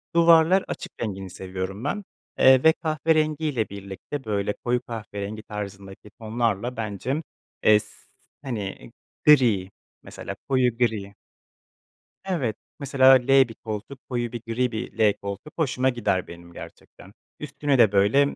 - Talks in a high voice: No, low, 115 Hz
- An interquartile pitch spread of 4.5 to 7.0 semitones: Yes, average, 5.1 semitones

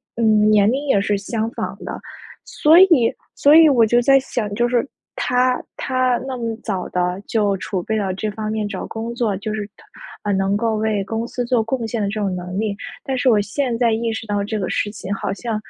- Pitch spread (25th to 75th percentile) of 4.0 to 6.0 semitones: No, average, 2.9 semitones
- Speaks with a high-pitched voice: Yes, high, 220 Hz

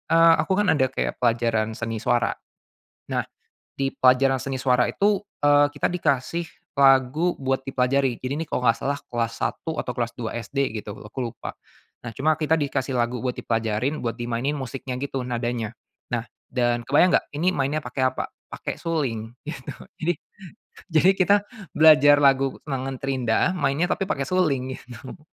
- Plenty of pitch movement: No, average, 3.5 semitones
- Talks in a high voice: No, low, 135 Hz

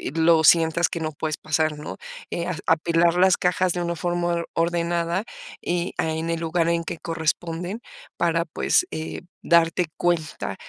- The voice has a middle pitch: Yes, medium, 170 Hz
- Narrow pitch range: Yes, narrow, 1.2 semitones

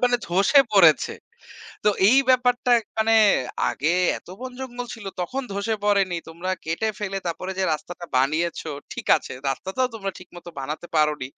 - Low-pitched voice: No, high, 190 Hz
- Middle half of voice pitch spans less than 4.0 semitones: No, wide, 5.4 semitones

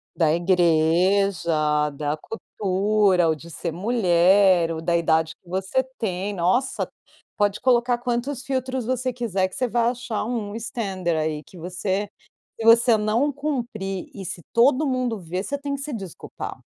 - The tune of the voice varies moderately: No, wide, 5.8 semitones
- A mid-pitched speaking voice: No, high, 200 Hz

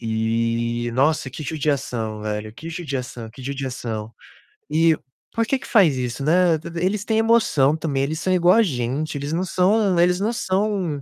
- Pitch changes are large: Yes, wide, 6.7 semitones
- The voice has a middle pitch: Yes, medium, 150 Hz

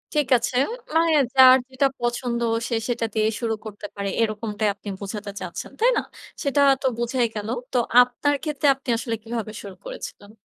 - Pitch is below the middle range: No, high, 235 Hz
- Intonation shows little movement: No, average, 3.6 semitones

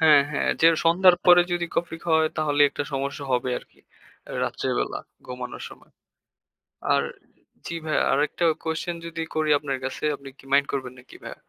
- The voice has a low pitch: No, medium, 150 Hz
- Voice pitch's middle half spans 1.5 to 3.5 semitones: Yes, average, 3.0 semitones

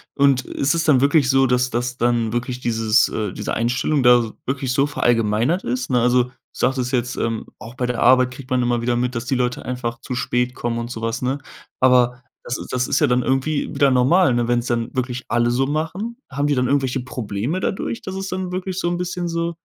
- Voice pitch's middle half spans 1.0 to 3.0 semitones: Yes, narrow, 2.6 semitones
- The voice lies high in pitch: No, low, 125 Hz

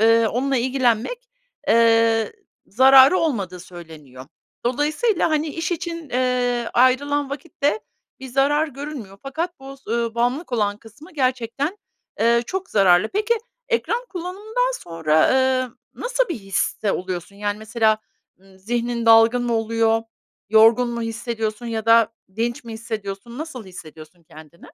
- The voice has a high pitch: Yes, high, 235 Hz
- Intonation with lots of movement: No, average, 4.5 semitones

